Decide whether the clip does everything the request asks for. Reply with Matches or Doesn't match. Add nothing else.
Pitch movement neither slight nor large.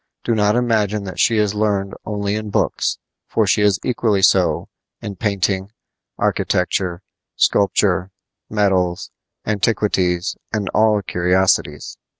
Doesn't match